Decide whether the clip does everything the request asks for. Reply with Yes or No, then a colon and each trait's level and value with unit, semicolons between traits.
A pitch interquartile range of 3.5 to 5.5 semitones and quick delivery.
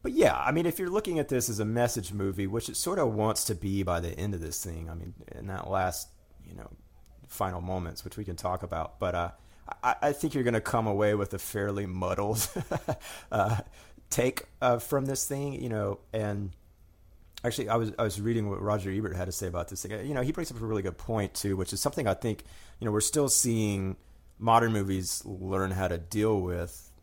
Yes: average, 3.9 semitones; fast, 235 wpm